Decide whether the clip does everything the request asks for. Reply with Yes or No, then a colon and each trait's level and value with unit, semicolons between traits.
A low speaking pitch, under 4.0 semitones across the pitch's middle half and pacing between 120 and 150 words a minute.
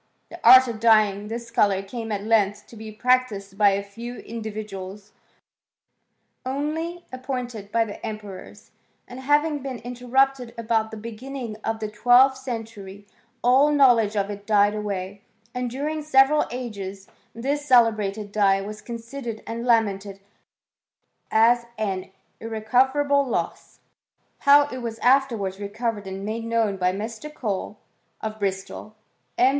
No: high, 225 Hz; average, 3.6 semitones; average, 140 wpm